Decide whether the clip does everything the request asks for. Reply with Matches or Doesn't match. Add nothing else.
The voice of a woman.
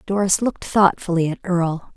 Matches